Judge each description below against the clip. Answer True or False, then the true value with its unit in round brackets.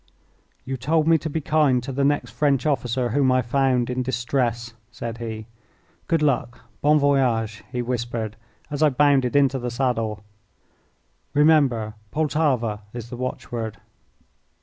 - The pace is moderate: True (145 wpm)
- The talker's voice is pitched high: False (130 Hz)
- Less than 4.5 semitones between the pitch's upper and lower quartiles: True (3.3 semitones)